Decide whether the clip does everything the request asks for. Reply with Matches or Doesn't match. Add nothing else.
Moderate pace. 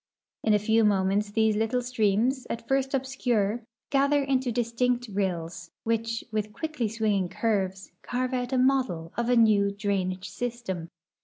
Matches